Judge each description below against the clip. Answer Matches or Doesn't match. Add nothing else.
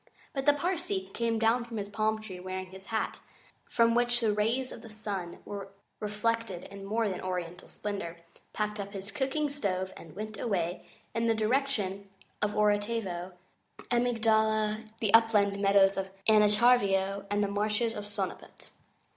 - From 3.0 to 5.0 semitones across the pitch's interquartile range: Doesn't match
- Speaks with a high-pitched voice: Matches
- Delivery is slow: Doesn't match